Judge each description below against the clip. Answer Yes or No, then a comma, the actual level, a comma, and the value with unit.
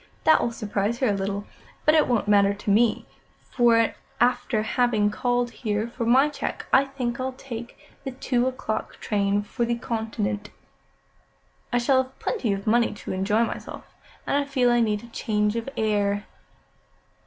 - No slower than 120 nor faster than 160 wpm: No, average, 170 wpm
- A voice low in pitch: No, high, 230 Hz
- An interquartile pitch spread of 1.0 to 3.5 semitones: Yes, average, 3.1 semitones